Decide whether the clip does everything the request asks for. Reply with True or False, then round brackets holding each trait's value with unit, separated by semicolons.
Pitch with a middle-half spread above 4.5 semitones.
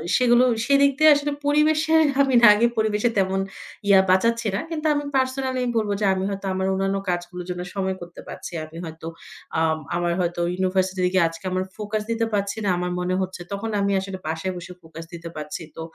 True (4.9 semitones)